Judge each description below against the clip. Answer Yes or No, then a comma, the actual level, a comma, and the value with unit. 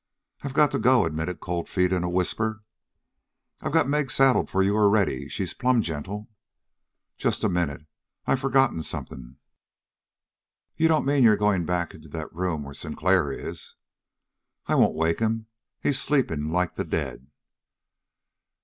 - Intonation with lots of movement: Yes, wide, 7.3 semitones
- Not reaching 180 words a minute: Yes, average, 150 wpm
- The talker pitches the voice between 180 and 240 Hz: No, very low, 95 Hz